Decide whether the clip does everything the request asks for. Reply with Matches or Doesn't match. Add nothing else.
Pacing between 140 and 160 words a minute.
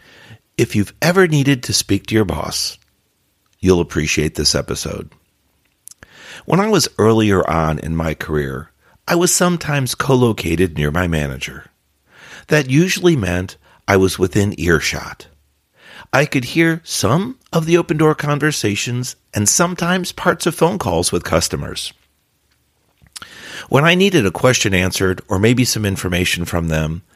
Matches